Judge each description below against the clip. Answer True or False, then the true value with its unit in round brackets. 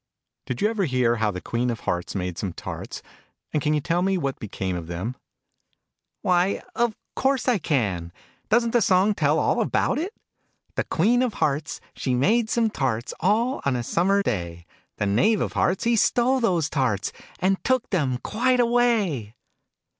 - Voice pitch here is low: False (170 Hz)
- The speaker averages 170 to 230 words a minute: True (180 wpm)